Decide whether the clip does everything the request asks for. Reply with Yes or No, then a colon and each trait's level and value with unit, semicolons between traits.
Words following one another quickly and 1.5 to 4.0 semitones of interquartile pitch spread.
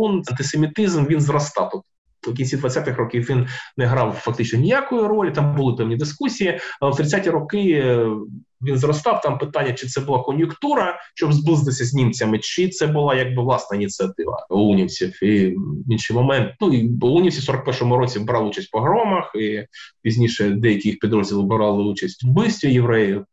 No: fast, 170 wpm; average, 5.2 semitones